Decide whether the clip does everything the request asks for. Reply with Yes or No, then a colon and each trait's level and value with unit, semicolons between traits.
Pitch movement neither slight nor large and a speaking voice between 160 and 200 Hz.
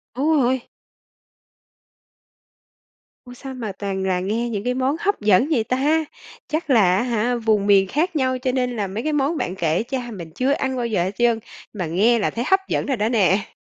No: average, 4.6 semitones; high, 240 Hz